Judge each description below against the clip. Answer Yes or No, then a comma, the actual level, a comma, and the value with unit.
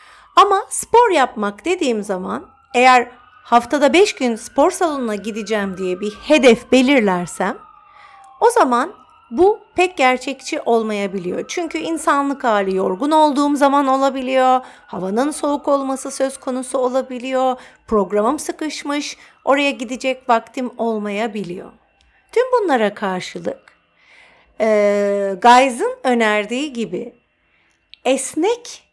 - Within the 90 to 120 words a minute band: Yes, average, 100 wpm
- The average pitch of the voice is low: No, very high, 260 Hz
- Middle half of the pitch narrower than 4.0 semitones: No, average, 5.3 semitones